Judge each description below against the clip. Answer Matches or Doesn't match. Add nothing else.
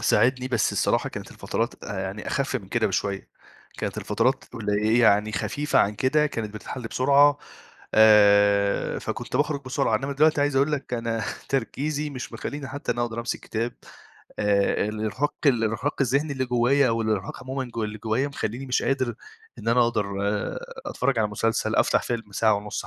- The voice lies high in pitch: Doesn't match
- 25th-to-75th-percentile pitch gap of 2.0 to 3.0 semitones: Doesn't match